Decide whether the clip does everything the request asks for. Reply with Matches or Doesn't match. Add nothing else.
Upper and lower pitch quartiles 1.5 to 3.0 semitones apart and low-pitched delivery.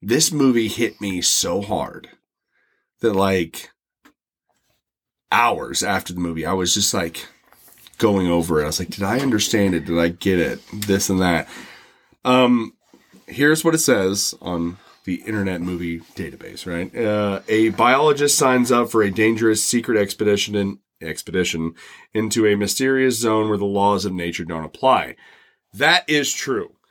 Doesn't match